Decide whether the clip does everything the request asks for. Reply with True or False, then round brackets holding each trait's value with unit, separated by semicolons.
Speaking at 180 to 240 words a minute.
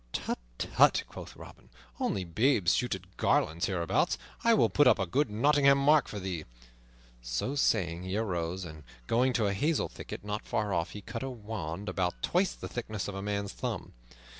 True (190 wpm)